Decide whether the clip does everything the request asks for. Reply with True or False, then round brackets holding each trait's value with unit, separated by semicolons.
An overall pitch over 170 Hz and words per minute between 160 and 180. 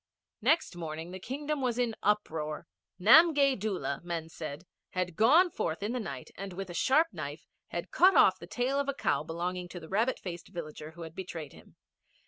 False (190 Hz; 195 wpm)